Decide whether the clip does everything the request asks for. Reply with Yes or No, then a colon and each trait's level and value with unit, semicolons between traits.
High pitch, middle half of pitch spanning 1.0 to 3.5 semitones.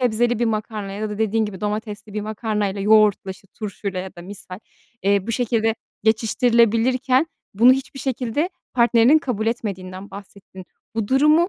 Yes: high, 220 Hz; average, 3.0 semitones